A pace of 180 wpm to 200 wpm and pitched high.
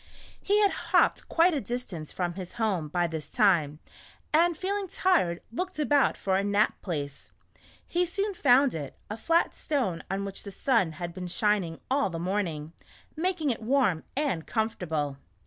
No: average, 170 wpm; high, 210 Hz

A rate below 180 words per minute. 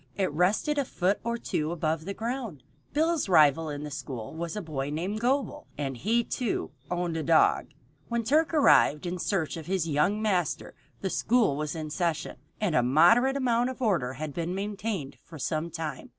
No: average, 190 wpm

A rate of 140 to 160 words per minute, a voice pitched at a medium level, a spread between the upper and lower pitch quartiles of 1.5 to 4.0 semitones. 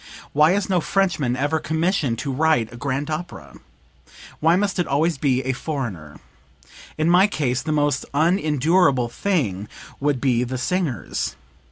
No: average, 150 wpm; medium, 145 Hz; average, 4.8 semitones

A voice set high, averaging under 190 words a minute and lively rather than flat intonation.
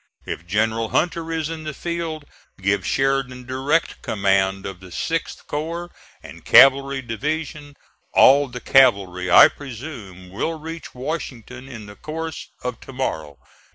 No: low, 130 Hz; average, 140 wpm; wide, 7.1 semitones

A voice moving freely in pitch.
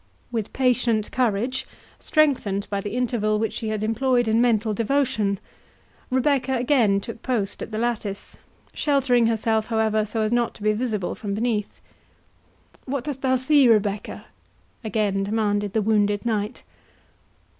No: average, 3.0 semitones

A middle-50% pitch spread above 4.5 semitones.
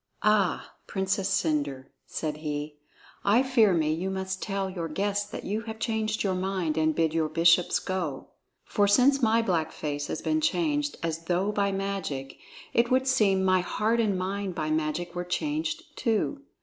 Yes: average, 4.9 semitones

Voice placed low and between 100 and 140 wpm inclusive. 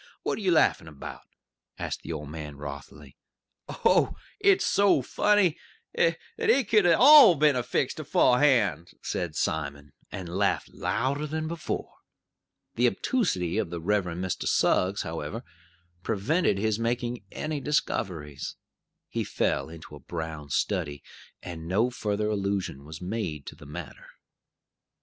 Yes: low, 100 Hz; slow, 135 wpm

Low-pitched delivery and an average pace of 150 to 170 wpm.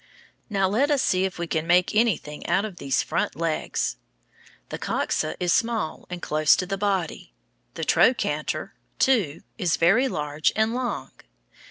No: medium, 185 Hz; average, 160 wpm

